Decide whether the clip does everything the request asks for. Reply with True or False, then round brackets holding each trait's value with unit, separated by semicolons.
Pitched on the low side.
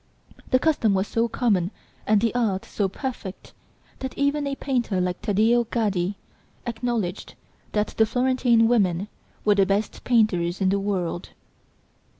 False (215 Hz)